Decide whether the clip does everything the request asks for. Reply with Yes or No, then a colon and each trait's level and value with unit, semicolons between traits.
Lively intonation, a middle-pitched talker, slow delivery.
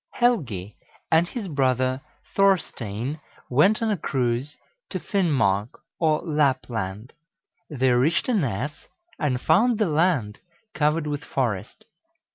Yes: wide, 5.7 semitones; medium, 145 Hz; slow, 115 wpm